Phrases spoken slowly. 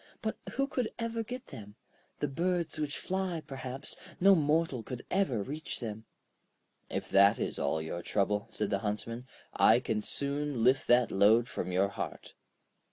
No: average, 165 wpm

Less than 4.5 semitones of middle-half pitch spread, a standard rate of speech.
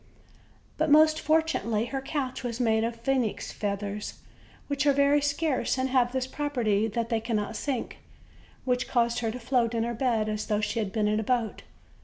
Yes: average, 3.5 semitones; average, 190 wpm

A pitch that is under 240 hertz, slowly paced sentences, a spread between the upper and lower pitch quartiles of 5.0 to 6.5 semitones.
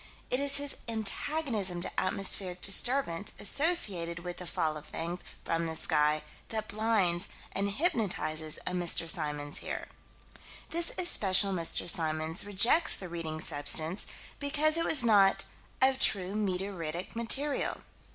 Yes: high, 190 Hz; slow, 130 wpm; wide, 5.6 semitones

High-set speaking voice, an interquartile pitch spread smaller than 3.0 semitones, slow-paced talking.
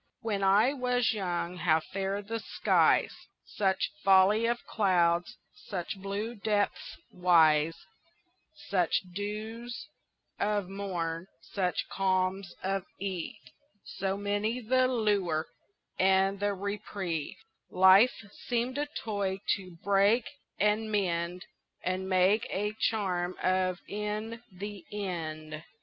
Yes: high, 195 Hz; narrow, 2.6 semitones; slow, 110 wpm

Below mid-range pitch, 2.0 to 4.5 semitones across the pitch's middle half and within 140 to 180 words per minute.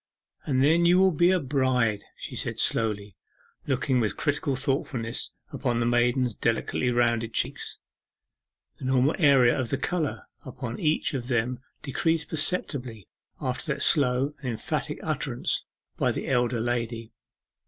Yes: low, 125 Hz; average, 3.3 semitones; average, 145 wpm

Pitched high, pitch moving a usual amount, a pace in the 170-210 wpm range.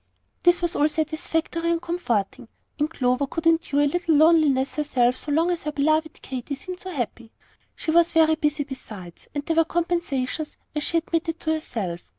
Yes: very high, 310 Hz; average, 3.3 semitones; average, 180 wpm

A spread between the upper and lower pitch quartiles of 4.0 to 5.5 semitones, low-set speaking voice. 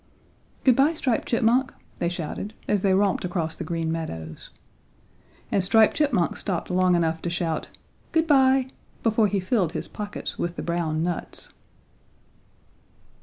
No: average, 5.0 semitones; medium, 185 Hz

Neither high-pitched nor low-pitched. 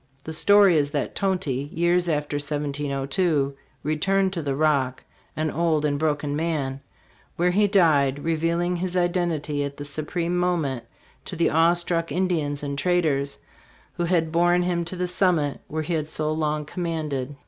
Yes: medium, 160 Hz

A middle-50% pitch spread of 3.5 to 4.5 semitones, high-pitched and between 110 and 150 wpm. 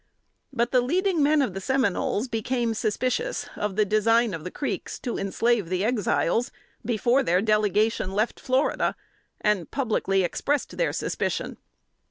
Yes: average, 4.0 semitones; high, 225 Hz; average, 145 wpm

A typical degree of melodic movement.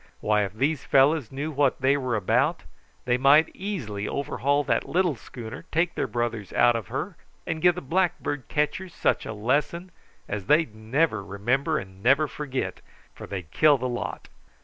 No: wide, 5.7 semitones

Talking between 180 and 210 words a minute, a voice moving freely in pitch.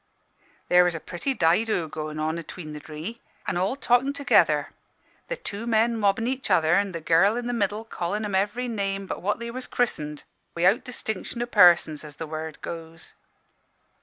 Yes: average, 185 wpm; wide, 6.1 semitones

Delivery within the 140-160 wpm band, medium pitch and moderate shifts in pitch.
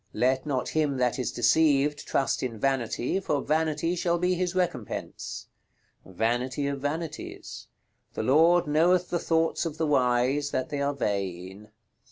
Yes: average, 150 wpm; medium, 145 Hz; average, 4.4 semitones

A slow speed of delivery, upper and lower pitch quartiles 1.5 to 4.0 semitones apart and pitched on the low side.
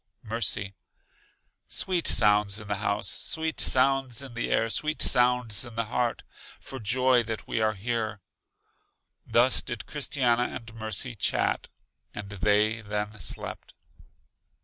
Yes: slow, 130 wpm; average, 2.9 semitones; low, 115 Hz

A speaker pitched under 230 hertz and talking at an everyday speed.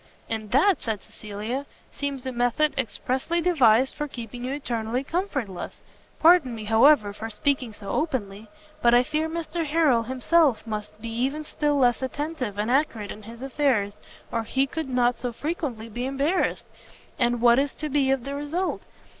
No: very high, 255 Hz; average, 165 wpm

